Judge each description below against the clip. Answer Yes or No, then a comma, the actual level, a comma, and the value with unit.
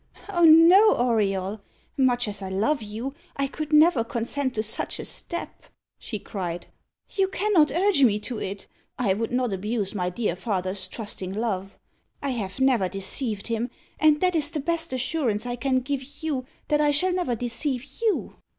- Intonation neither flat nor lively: No, wide, 6.4 semitones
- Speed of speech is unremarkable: Yes, average, 175 wpm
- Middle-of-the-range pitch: No, high, 245 Hz